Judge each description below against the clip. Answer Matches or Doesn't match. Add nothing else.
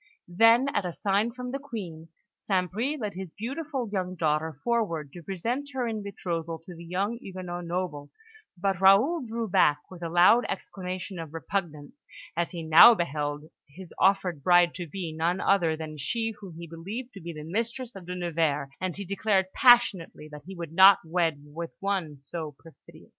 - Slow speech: Doesn't match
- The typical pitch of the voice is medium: Matches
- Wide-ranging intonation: Doesn't match